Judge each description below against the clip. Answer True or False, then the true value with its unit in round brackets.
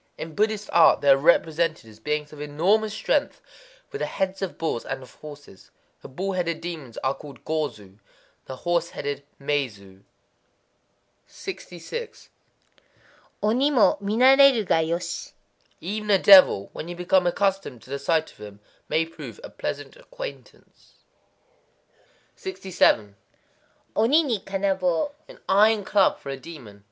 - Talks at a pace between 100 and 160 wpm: True (145 wpm)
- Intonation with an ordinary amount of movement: False (6.2 semitones)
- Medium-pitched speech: True (170 Hz)